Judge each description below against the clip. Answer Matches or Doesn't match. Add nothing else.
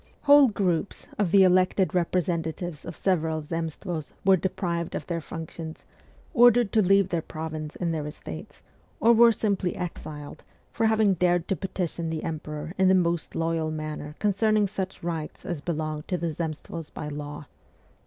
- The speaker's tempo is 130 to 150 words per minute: Doesn't match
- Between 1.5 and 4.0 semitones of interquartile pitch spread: Matches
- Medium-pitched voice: Matches